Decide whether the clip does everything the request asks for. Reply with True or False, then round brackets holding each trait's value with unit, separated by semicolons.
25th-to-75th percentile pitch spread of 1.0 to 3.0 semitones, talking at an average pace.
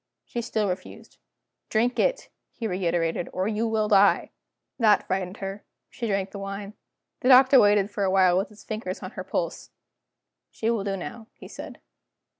True (2.7 semitones; 175 wpm)